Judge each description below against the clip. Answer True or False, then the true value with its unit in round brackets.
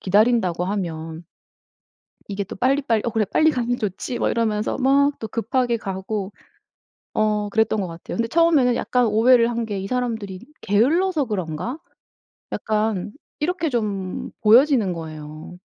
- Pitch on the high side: True (220 Hz)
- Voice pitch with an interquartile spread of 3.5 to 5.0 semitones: True (4.3 semitones)